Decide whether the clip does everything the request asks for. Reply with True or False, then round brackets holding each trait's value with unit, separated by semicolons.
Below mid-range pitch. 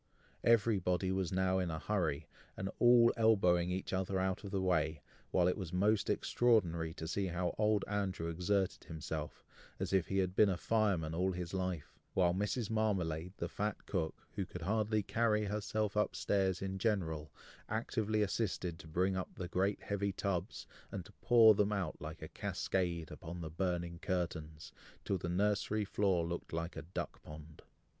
True (95 Hz)